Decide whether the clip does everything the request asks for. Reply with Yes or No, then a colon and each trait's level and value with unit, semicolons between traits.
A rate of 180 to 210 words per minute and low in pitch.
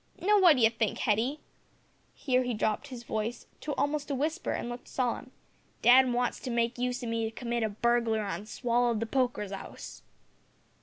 No: average, 185 wpm; high, 240 Hz